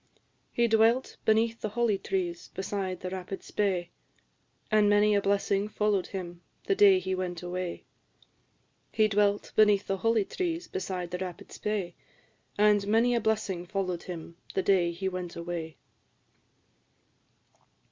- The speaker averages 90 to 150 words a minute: Yes, average, 140 wpm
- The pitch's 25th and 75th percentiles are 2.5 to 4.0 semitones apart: Yes, average, 2.9 semitones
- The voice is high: Yes, high, 195 Hz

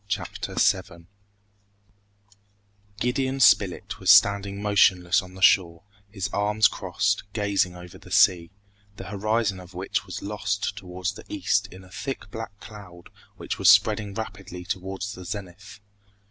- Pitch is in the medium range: No, low, 100 Hz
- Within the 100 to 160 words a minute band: Yes, average, 140 wpm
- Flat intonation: Yes, narrow, 2.2 semitones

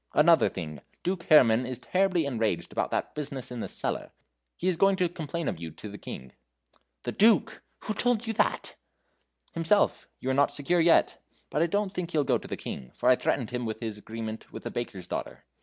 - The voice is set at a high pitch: No, medium, 145 Hz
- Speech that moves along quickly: Yes, fast, 215 wpm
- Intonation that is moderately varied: No, wide, 7.9 semitones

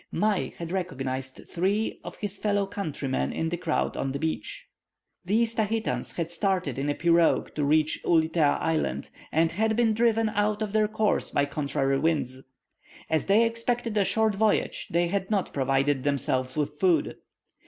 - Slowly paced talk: No, average, 165 wpm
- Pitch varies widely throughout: Yes, wide, 6.4 semitones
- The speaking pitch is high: No, medium, 175 Hz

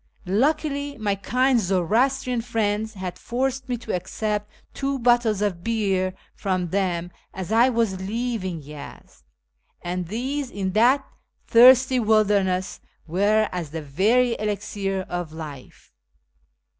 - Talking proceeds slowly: Yes, slow, 120 wpm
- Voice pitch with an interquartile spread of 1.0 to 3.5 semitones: No, average, 4.7 semitones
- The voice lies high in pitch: Yes, high, 210 Hz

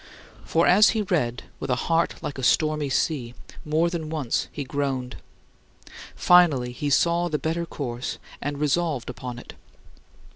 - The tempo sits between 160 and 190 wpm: No, average, 150 wpm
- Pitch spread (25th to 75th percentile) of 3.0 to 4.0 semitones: No, average, 4.7 semitones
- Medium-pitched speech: Yes, medium, 150 Hz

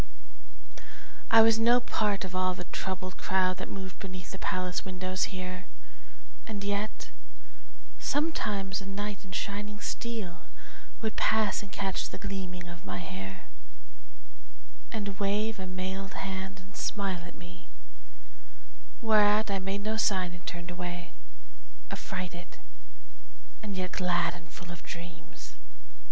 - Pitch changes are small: Yes, narrow, 2.3 semitones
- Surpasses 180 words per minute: No, slow, 135 wpm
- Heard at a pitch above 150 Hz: Yes, high, 190 Hz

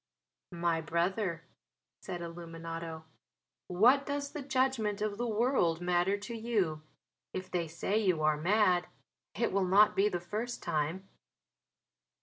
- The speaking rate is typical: No, slow, 130 wpm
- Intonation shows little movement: No, average, 4.6 semitones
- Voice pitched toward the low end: No, high, 190 Hz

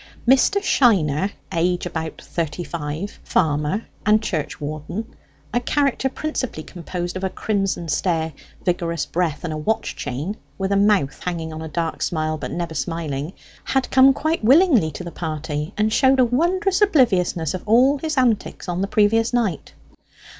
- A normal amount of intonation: No, wide, 7.0 semitones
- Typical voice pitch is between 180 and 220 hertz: Yes, medium, 185 Hz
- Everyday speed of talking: Yes, average, 160 wpm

